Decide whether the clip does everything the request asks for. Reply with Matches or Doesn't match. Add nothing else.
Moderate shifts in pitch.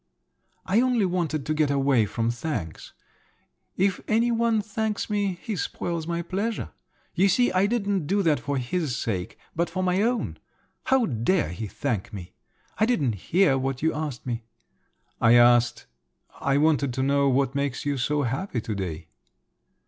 Doesn't match